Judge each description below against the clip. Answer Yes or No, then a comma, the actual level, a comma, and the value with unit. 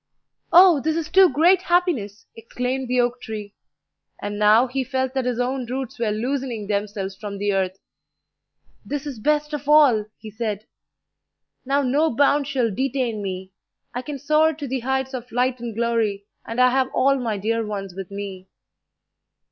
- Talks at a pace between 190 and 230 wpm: No, average, 170 wpm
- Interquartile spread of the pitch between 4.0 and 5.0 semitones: Yes, average, 4.6 semitones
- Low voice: No, very high, 250 Hz